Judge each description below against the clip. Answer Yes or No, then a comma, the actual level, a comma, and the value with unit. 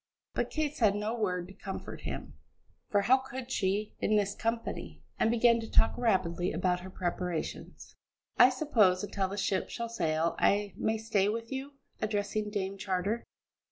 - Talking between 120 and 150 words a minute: No, average, 165 wpm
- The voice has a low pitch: No, high, 205 Hz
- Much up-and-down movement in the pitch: No, average, 3.4 semitones